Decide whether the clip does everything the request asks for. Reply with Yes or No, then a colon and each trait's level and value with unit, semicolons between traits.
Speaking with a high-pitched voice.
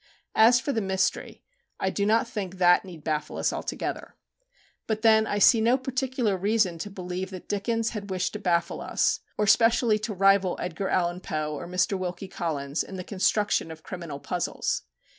Yes: high, 195 Hz